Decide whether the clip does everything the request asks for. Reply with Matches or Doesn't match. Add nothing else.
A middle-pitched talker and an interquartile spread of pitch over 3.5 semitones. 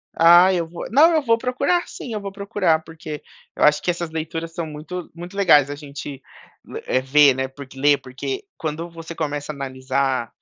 Matches